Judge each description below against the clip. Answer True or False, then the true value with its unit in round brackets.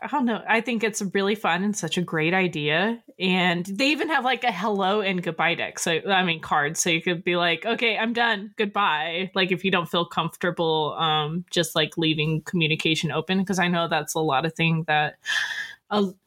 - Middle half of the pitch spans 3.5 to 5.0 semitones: True (4.3 semitones)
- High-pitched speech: False (180 Hz)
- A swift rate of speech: True (215 wpm)